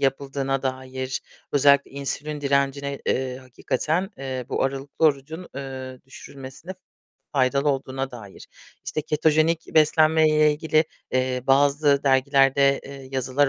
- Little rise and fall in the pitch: Yes, narrow, 2.0 semitones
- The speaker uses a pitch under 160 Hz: Yes, medium, 140 Hz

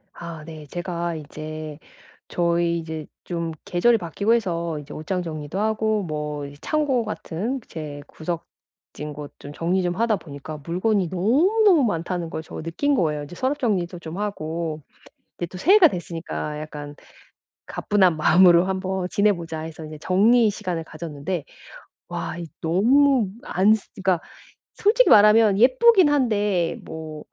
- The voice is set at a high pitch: No, medium, 175 Hz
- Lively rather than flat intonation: No, average, 4.9 semitones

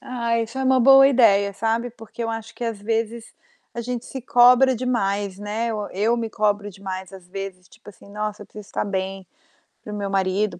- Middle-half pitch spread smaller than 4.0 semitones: Yes, average, 2.9 semitones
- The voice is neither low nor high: No, high, 215 Hz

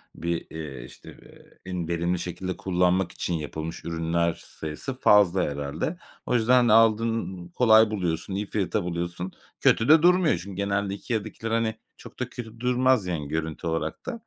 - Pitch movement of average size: Yes, average, 5.0 semitones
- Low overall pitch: Yes, very low, 95 Hz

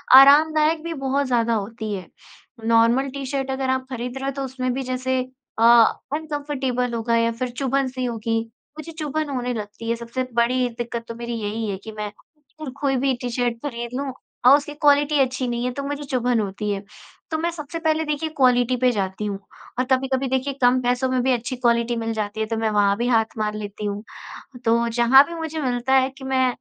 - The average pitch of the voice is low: No, very high, 250 Hz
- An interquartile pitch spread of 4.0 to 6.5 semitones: No, average, 2.8 semitones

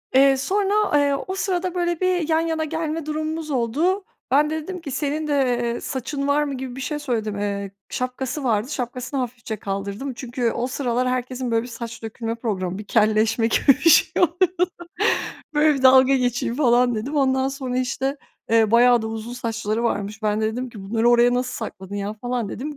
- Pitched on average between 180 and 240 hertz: No, very high, 255 Hz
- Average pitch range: Yes, average, 4.5 semitones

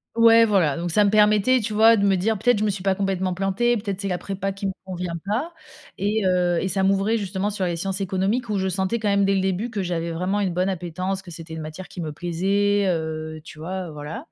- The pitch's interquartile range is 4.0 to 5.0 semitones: No, narrow, 2.5 semitones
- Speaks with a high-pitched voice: Yes, high, 195 Hz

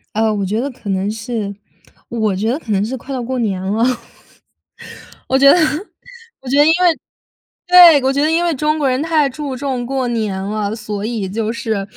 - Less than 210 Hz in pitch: No, high, 245 Hz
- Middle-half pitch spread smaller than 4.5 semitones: No, wide, 5.4 semitones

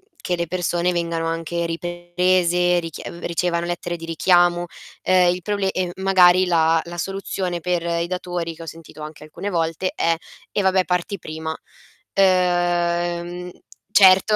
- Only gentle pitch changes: Yes, narrow, 1.4 semitones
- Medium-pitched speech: Yes, medium, 175 Hz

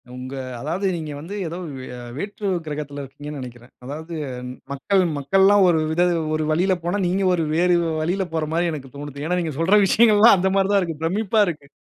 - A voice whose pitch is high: No, medium, 170 Hz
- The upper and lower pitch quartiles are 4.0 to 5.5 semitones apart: Yes, average, 4.6 semitones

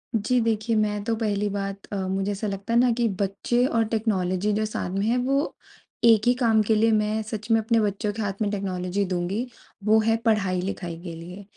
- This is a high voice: Yes, high, 210 Hz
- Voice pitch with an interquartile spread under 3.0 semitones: Yes, narrow, 2.4 semitones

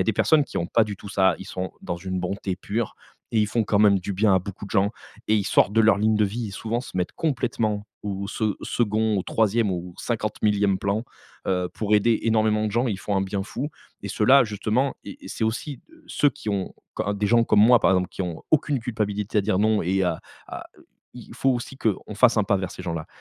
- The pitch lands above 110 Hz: No, low, 105 Hz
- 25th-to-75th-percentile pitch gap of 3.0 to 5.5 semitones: No, narrow, 2.6 semitones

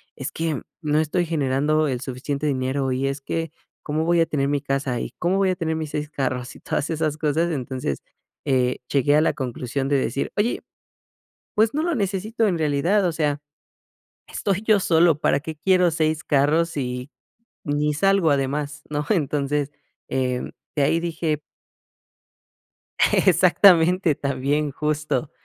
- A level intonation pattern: No, average, 3.2 semitones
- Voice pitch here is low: No, medium, 150 Hz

